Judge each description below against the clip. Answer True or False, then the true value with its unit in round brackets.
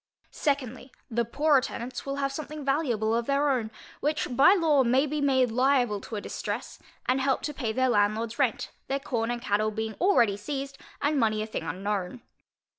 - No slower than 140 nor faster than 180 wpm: False (190 wpm)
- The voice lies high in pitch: True (255 Hz)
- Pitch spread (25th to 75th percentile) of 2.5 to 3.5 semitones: False (4.1 semitones)